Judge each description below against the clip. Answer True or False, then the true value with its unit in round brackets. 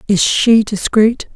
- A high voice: True (215 Hz)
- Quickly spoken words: False (135 wpm)